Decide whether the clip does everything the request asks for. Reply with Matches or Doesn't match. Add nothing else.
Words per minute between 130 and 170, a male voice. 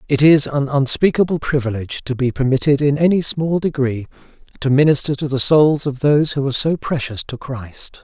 Doesn't match